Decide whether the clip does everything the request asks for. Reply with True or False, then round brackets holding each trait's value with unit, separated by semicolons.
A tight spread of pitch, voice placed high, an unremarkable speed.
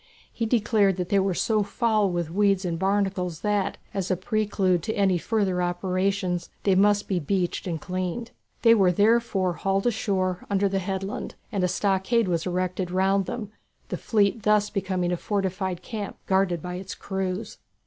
True (2.1 semitones; 195 Hz; 170 wpm)